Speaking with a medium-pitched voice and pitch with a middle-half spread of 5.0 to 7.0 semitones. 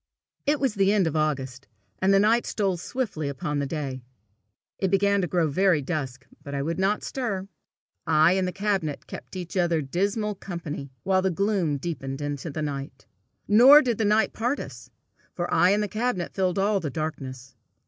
Yes: medium, 180 Hz; wide, 5.5 semitones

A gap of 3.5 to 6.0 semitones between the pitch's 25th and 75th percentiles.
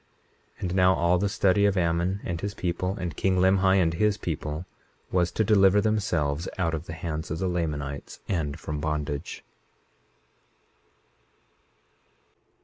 No: average, 3.1 semitones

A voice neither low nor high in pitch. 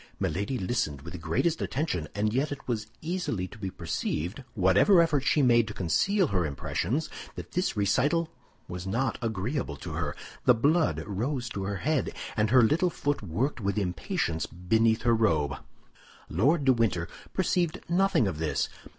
No: low, 115 Hz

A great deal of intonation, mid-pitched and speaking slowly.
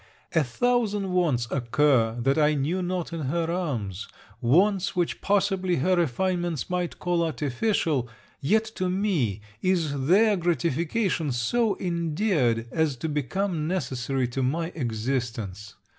Yes: wide, 6.1 semitones; medium, 160 Hz; slow, 130 wpm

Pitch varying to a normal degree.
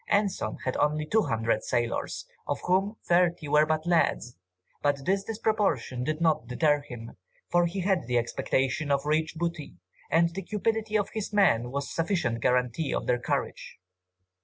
No: wide, 6.5 semitones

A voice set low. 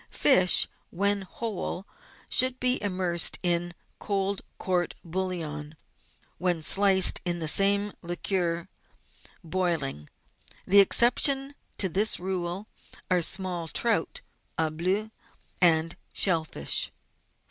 No: medium, 185 Hz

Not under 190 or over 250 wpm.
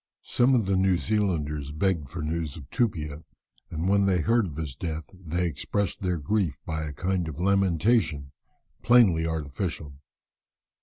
No: average, 155 wpm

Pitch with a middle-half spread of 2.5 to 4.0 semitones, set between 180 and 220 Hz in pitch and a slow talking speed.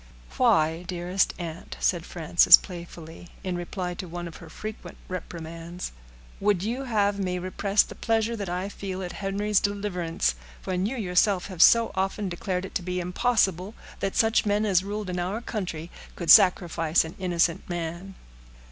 No: average, 2.8 semitones; medium, 185 Hz; average, 165 wpm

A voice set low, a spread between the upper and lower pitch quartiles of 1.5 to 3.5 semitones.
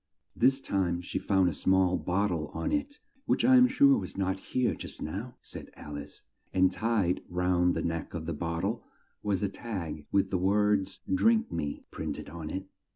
No: very low, 95 Hz; average, 4.7 semitones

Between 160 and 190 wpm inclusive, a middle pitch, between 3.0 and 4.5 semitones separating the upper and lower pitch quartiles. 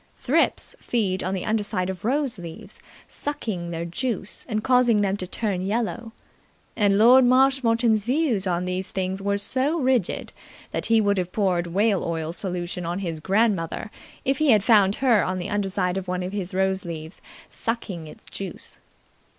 No: average, 170 wpm; high, 200 Hz; average, 4.0 semitones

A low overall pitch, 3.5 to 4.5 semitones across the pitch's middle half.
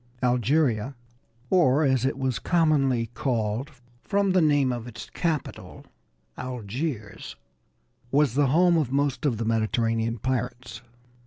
Yes: low, 130 Hz; average, 4.2 semitones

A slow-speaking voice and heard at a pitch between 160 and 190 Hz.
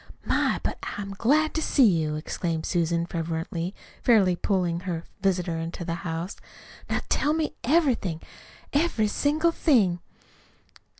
Yes: slow, 130 wpm; medium, 185 Hz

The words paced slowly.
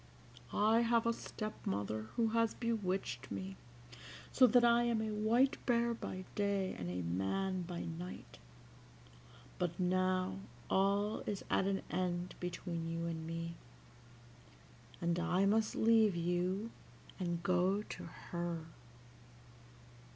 Yes: slow, 130 wpm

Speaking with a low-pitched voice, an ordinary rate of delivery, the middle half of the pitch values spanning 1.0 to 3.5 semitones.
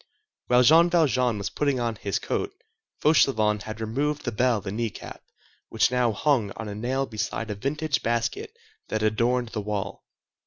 No: low, 120 Hz; average, 165 wpm; average, 4.1 semitones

